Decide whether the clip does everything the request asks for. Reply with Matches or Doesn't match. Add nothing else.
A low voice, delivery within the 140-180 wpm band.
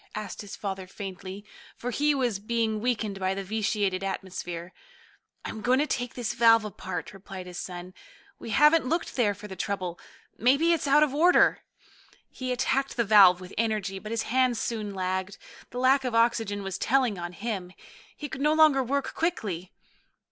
Doesn't match